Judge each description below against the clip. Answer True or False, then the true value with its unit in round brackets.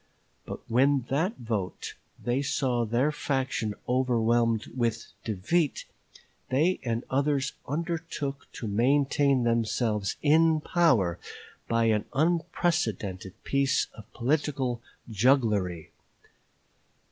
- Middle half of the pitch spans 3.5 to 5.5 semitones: True (4.2 semitones)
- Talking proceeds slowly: True (100 wpm)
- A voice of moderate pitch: False (130 Hz)